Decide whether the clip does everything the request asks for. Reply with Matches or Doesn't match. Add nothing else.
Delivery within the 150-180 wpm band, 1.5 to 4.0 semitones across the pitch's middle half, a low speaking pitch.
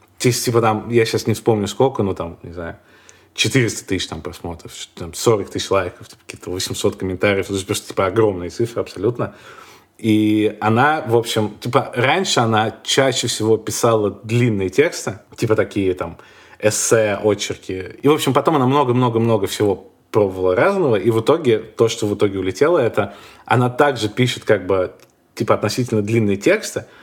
Matches